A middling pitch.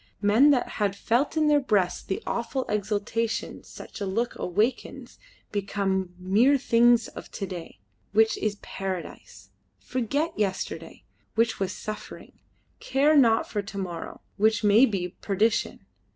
No: high, 215 Hz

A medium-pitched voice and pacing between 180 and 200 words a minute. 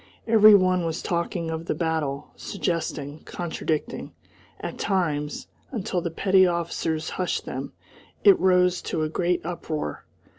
No: medium, 170 Hz; slow, 135 wpm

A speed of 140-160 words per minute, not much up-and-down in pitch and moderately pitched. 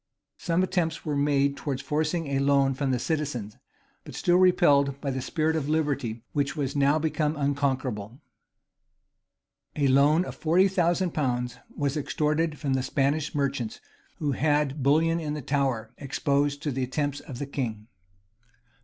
Yes: average, 155 wpm; narrow, 2.3 semitones; medium, 145 Hz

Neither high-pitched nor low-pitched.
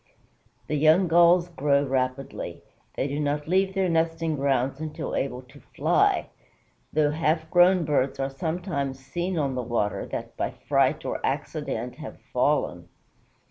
Yes: medium, 150 Hz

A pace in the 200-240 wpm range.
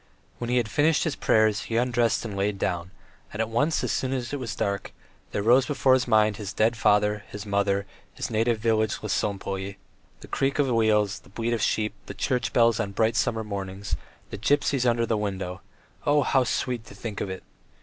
Yes: fast, 205 wpm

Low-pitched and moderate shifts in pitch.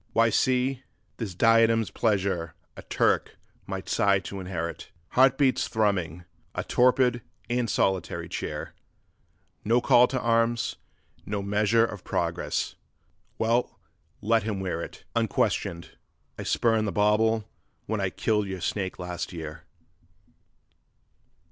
Yes: low, 110 Hz; average, 3.3 semitones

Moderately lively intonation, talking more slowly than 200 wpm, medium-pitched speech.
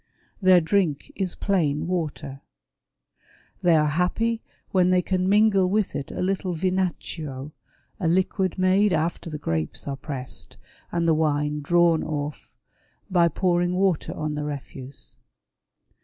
Yes: average, 3.8 semitones; slow, 135 wpm; medium, 170 Hz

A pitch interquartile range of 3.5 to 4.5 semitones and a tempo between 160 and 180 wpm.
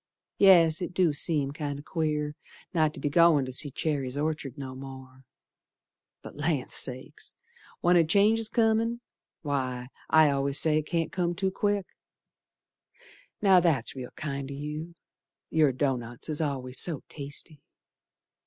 No: average, 3.8 semitones; average, 145 wpm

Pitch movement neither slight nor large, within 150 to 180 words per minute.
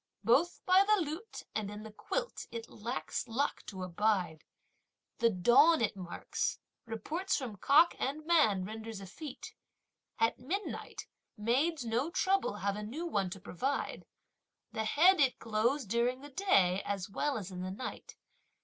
No: wide, 6.7 semitones; average, 155 wpm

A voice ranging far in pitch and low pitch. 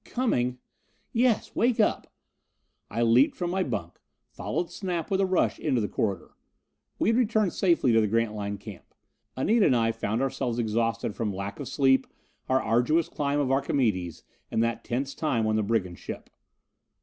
Yes: wide, 7.1 semitones; low, 125 Hz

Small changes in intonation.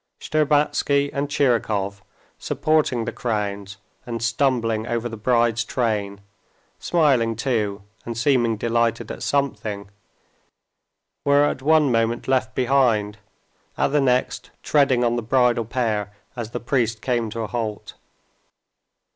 No: average, 3.2 semitones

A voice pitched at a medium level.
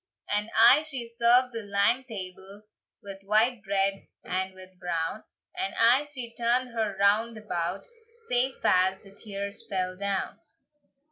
No: high, 210 Hz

